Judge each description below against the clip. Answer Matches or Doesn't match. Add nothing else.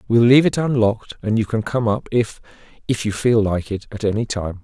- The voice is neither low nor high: Doesn't match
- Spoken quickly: Matches